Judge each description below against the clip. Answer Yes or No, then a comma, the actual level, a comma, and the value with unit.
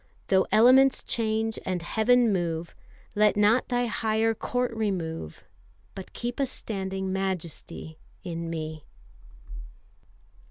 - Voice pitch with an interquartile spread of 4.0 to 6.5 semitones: Yes, average, 4.6 semitones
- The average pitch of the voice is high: Yes, high, 205 Hz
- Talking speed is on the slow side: Yes, slow, 110 wpm